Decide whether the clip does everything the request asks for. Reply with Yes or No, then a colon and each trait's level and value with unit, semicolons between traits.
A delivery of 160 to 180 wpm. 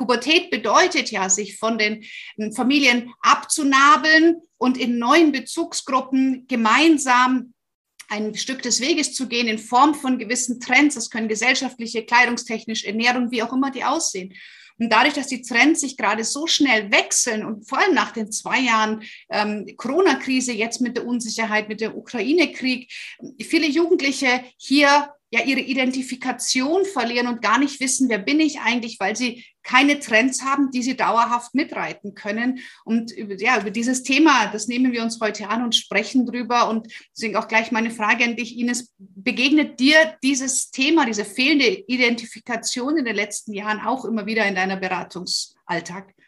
Yes: average, 165 wpm